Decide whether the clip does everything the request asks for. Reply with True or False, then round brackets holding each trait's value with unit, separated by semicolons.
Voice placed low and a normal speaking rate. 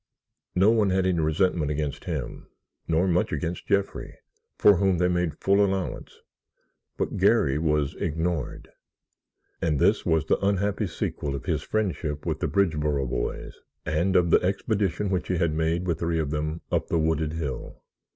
True (85 Hz; 165 wpm)